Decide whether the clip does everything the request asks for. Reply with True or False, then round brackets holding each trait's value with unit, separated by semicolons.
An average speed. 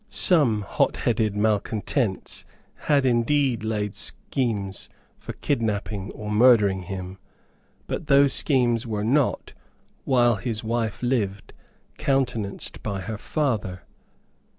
False (105 wpm)